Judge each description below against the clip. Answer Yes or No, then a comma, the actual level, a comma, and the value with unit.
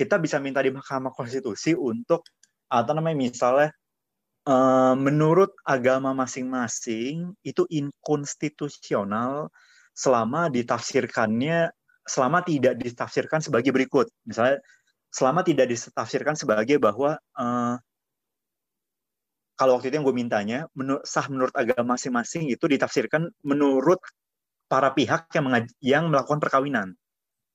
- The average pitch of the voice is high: No, low, 135 Hz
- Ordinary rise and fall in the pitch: Yes, average, 3.6 semitones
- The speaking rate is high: No, average, 105 wpm